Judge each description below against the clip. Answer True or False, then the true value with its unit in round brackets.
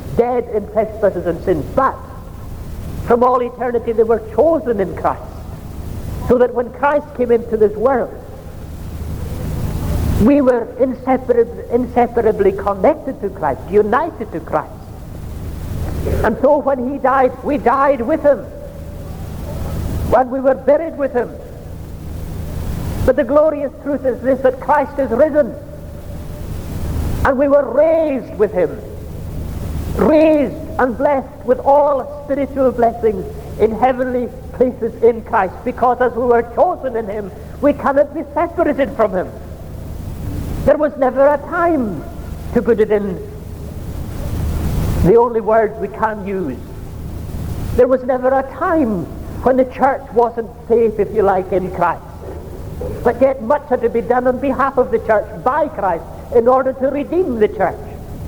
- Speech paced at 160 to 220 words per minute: False (140 wpm)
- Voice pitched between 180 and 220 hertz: False (230 Hz)